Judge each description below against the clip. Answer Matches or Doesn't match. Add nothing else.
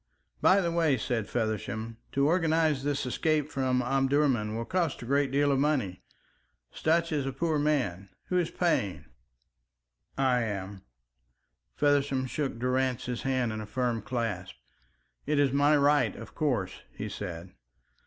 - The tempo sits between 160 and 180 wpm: Doesn't match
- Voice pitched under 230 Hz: Matches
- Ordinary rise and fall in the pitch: Matches